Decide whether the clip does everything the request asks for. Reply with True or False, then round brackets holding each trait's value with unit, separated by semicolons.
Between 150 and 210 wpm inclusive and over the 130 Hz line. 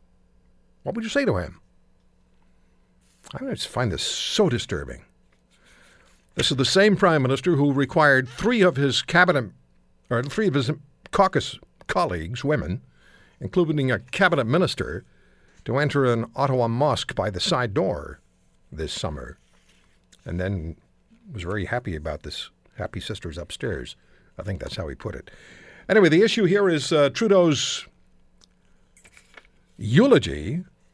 False (140 wpm; 140 Hz)